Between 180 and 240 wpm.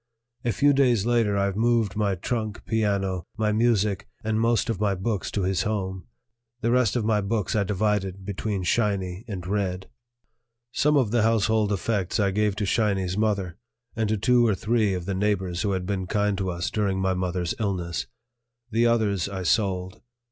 Yes: average, 185 wpm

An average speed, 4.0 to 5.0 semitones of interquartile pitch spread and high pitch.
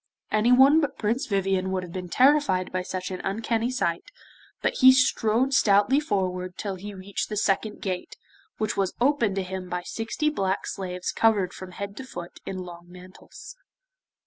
Yes: average, 170 wpm; average, 4.3 semitones; high, 200 Hz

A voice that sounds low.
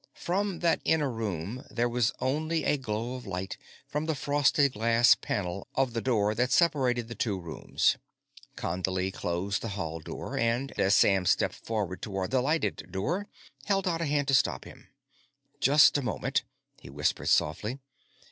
Yes: low, 120 Hz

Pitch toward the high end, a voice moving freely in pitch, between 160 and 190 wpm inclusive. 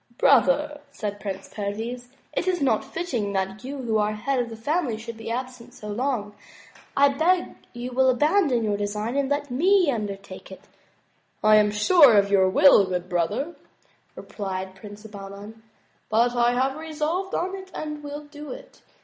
Yes: high, 240 Hz; wide, 5.8 semitones; average, 175 wpm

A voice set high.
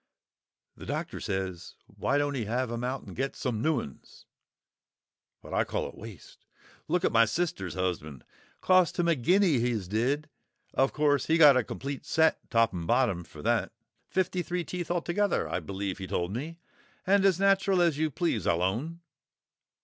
No: low, 135 Hz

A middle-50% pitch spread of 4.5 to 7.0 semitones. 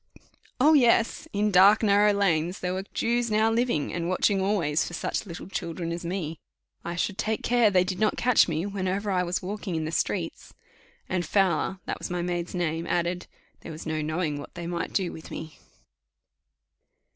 No: average, 3.4 semitones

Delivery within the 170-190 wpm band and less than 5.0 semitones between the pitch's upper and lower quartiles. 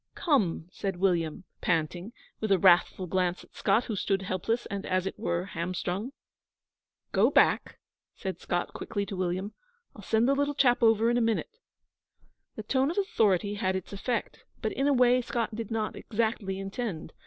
Yes: average, 175 wpm; average, 3.9 semitones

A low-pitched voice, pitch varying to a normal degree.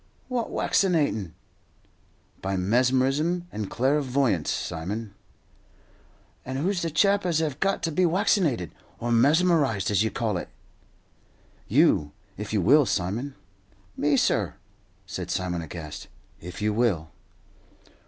No: low, 125 Hz; wide, 8.4 semitones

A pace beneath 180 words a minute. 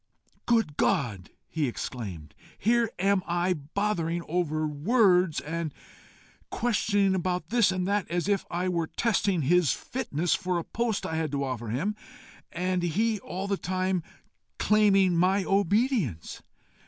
Yes: average, 140 wpm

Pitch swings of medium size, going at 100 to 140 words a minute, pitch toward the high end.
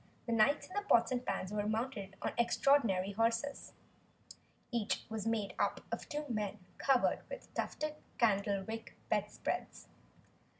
Yes: average, 4.2 semitones; slow, 135 wpm; high, 230 Hz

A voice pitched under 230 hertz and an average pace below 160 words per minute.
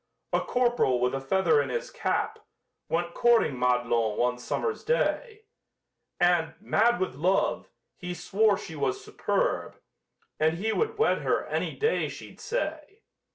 Yes: high, 190 Hz; average, 145 wpm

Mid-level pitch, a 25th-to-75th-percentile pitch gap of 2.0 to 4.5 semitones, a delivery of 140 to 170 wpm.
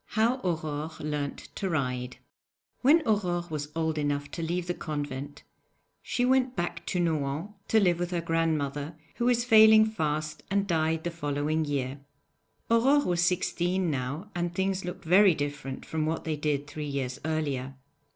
Yes: medium, 160 Hz; average, 4.1 semitones; average, 160 wpm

